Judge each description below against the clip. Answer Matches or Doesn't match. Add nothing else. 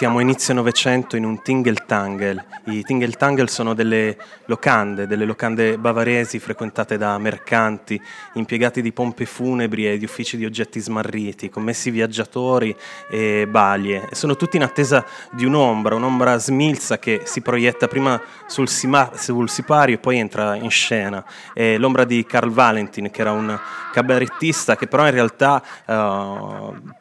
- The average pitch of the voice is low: Matches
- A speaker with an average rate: Matches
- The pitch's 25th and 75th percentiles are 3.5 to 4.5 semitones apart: Doesn't match